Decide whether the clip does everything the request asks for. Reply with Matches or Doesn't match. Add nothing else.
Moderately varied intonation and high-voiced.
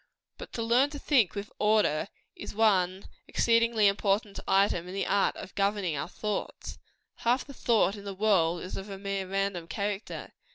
Doesn't match